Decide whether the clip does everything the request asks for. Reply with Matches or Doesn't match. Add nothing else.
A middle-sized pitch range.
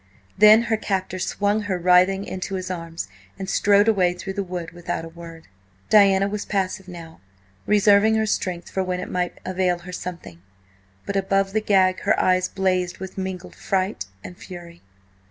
Doesn't match